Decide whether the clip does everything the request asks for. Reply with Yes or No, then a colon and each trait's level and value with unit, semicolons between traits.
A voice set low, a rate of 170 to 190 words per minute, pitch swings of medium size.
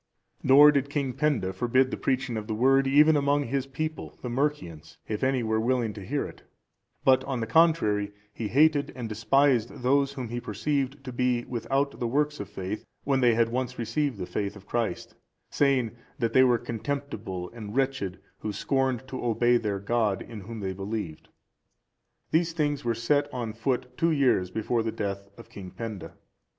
Yes: low, 120 Hz; average, 185 wpm; average, 4.2 semitones